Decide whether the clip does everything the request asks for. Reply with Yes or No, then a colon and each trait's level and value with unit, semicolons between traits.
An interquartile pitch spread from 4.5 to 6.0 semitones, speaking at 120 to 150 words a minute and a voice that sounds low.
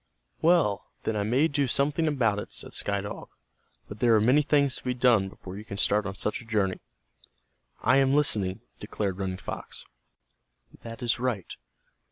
No: average, 4.9 semitones; average, 180 wpm; low, 115 Hz